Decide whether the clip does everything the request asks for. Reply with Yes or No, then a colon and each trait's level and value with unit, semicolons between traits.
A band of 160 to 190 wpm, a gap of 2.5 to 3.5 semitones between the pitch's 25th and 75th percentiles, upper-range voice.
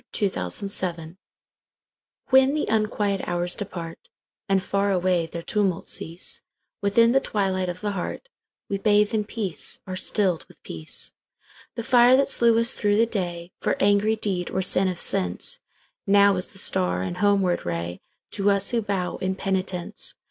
No: average, 150 wpm; average, 2.9 semitones; high, 195 Hz